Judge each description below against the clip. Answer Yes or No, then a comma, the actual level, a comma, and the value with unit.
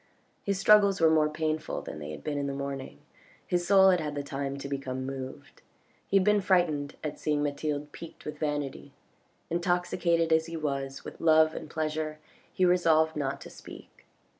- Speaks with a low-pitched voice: No, medium, 155 Hz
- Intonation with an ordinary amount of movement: Yes, average, 3.3 semitones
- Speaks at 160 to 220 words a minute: Yes, average, 185 wpm